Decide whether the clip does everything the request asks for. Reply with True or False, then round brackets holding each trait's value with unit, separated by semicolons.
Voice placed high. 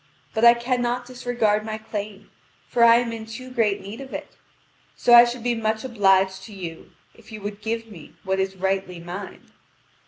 True (220 Hz)